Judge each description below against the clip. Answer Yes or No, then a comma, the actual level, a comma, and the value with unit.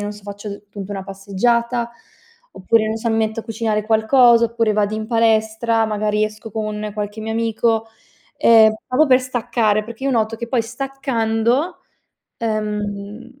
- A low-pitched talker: No, high, 220 Hz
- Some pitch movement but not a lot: No, narrow, 1.7 semitones